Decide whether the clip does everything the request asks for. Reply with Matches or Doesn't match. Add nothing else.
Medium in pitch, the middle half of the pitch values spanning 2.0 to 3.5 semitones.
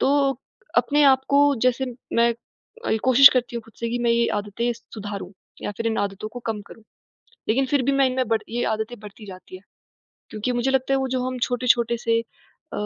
Doesn't match